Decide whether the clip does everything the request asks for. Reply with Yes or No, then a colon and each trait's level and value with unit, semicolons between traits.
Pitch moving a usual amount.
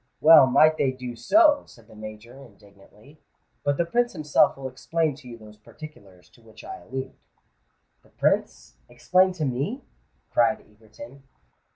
No: wide, 6.0 semitones